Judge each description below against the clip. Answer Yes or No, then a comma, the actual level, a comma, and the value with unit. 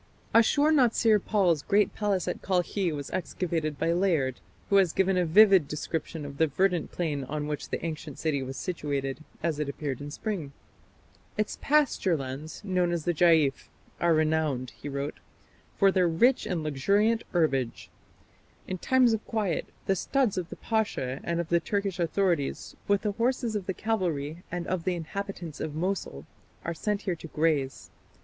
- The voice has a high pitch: No, medium, 170 Hz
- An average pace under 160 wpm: No, average, 170 wpm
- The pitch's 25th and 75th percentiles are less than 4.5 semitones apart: No, average, 4.8 semitones